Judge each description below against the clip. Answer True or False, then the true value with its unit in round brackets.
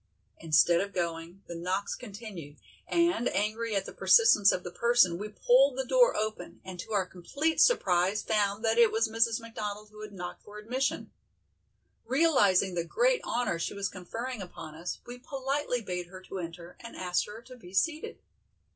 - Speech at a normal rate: True (180 wpm)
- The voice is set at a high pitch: True (210 Hz)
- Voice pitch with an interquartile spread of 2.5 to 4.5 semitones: False (5.2 semitones)